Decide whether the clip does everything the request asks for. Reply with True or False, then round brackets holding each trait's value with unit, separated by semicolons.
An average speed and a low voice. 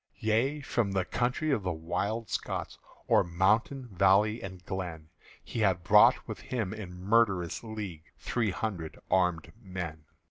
True (145 wpm; 95 Hz)